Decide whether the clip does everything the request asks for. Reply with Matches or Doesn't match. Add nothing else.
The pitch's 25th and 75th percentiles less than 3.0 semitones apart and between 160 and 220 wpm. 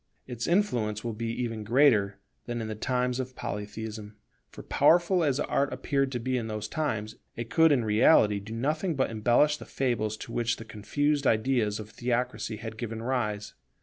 Doesn't match